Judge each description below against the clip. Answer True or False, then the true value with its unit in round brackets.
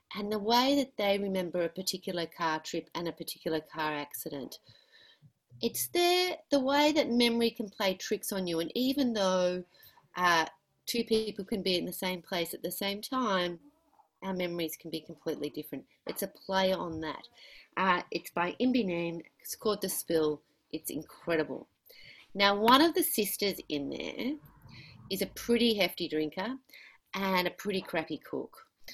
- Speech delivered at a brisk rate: False (170 wpm)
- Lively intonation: True (5.7 semitones)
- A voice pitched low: False (190 Hz)